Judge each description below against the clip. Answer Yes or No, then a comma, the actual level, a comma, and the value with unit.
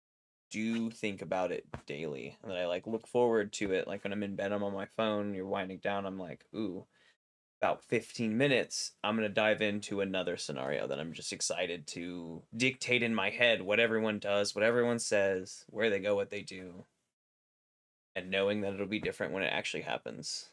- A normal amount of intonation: No, narrow, 2.3 semitones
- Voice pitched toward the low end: Yes, low, 100 Hz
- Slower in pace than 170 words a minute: No, average, 200 wpm